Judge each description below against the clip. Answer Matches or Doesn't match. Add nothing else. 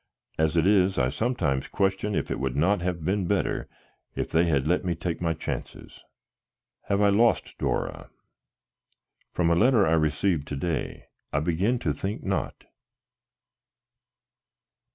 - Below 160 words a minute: Matches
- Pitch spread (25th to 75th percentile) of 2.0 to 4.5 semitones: Matches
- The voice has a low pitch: Matches